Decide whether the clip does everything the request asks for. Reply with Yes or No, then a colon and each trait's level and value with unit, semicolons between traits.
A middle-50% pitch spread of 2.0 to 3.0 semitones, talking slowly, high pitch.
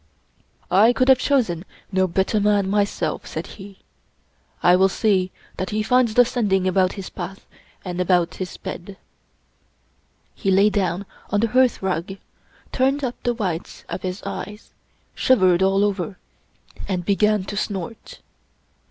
No: narrow, 2.5 semitones; average, 145 wpm; high, 195 Hz